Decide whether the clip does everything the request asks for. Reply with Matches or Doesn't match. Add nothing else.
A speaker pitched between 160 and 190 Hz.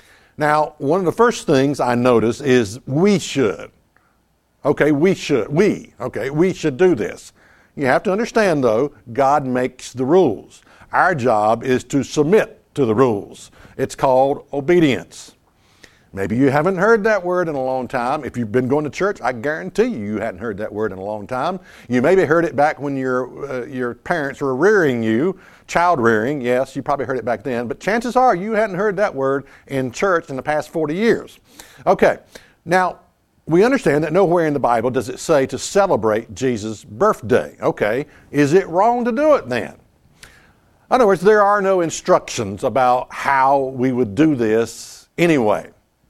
Doesn't match